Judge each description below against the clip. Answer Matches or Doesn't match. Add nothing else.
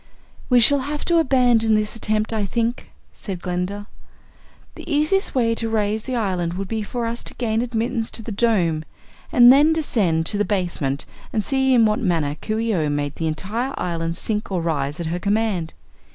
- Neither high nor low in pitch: Doesn't match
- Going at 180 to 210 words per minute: Matches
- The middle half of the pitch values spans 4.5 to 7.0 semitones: Matches